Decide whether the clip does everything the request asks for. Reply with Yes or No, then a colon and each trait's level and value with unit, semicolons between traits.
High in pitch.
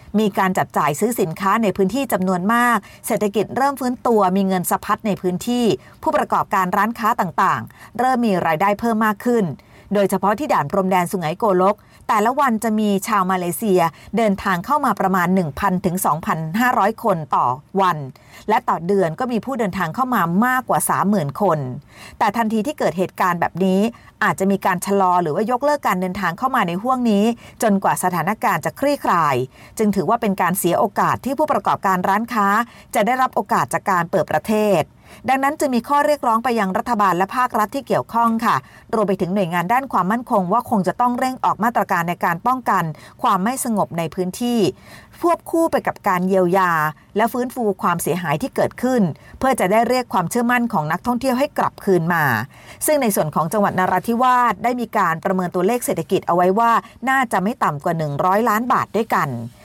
Yes: high, 200 Hz